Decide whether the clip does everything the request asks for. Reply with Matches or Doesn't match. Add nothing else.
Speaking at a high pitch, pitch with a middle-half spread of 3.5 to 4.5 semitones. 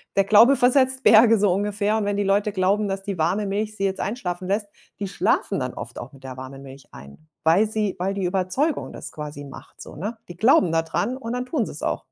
Matches